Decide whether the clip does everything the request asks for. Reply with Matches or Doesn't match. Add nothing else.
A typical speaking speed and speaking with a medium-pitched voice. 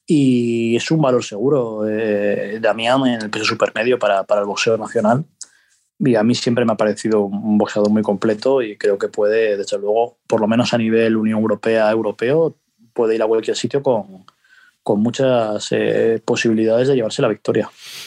Doesn't match